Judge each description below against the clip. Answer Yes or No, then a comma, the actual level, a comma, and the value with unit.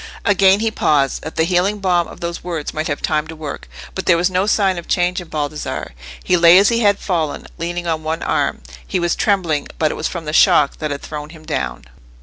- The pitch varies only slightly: No, average, 3.1 semitones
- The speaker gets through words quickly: Yes, fast, 235 wpm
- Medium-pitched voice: Yes, medium, 170 Hz